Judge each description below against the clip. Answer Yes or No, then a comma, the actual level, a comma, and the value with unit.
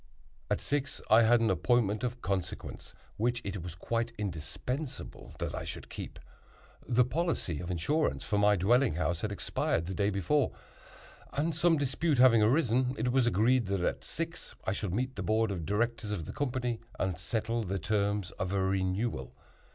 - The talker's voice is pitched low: Yes, low, 110 Hz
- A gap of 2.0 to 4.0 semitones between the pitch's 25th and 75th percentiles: No, average, 4.7 semitones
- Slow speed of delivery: No, average, 175 wpm